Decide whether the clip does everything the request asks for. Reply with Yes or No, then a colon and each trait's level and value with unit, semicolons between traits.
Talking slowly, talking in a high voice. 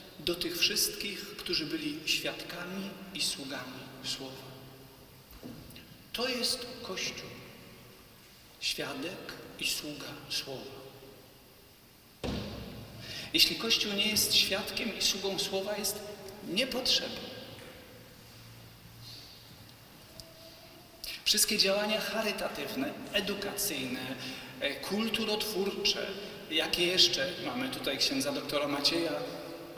Yes: slow, 75 wpm; high, 195 Hz